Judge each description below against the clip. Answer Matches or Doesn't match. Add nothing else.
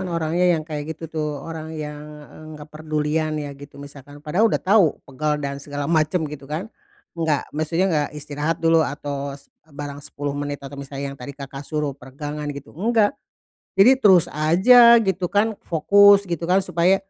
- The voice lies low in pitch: Doesn't match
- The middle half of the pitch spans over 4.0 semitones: Doesn't match